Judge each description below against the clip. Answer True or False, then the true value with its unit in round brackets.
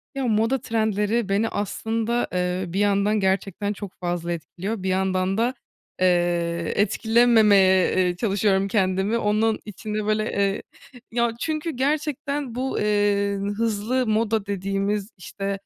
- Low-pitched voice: False (205 Hz)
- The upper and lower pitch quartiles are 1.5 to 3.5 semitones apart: True (2.9 semitones)